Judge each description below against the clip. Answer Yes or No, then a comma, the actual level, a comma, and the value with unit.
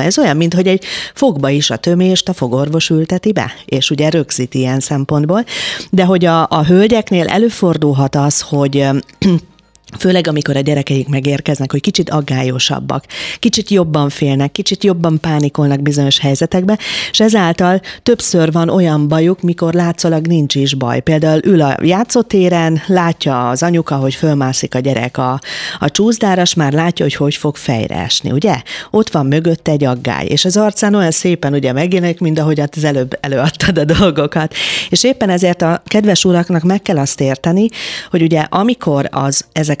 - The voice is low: No, medium, 160 Hz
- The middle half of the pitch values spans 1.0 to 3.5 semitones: No, average, 4.4 semitones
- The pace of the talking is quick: Yes, fast, 165 wpm